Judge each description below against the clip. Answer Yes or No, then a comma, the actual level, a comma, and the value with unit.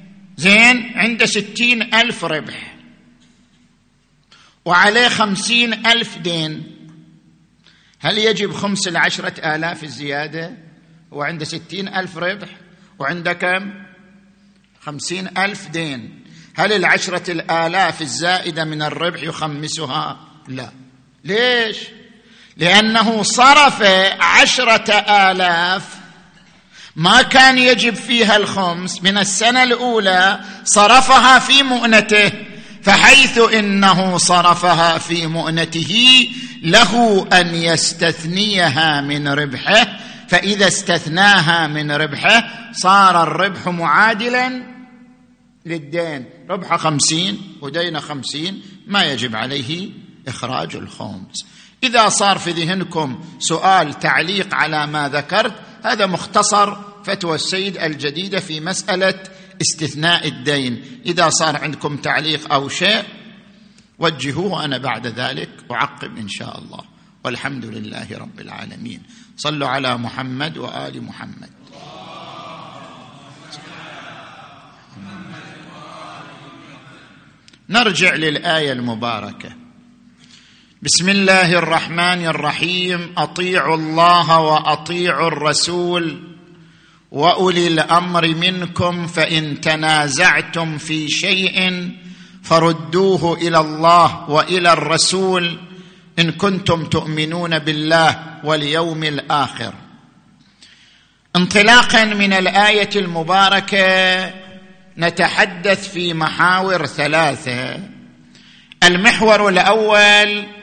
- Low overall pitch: No, medium, 180 Hz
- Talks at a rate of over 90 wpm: No, average, 85 wpm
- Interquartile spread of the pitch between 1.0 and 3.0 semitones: No, average, 4.1 semitones